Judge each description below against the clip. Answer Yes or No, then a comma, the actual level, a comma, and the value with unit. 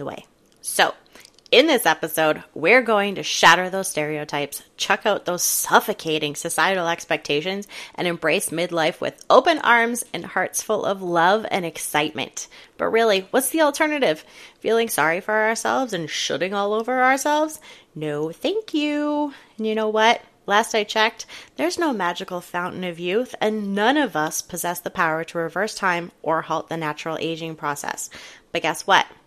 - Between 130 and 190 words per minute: Yes, average, 160 wpm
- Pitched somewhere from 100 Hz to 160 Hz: No, high, 190 Hz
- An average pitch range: No, wide, 5.9 semitones